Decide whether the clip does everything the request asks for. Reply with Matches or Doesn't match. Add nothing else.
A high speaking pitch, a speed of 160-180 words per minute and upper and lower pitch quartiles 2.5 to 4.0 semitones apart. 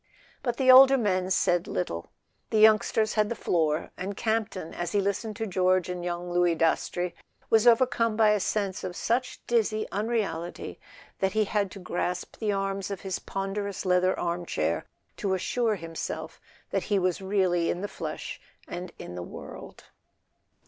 Matches